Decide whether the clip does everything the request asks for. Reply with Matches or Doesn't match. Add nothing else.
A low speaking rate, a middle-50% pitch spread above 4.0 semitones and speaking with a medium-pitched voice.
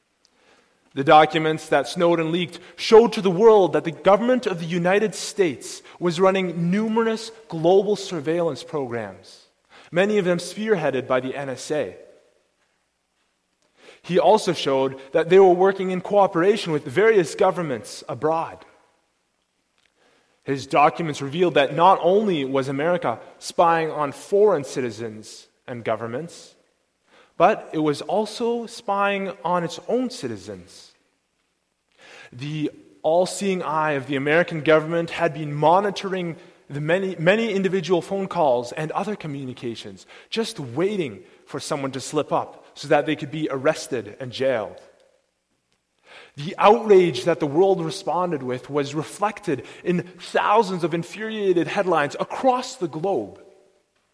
Matches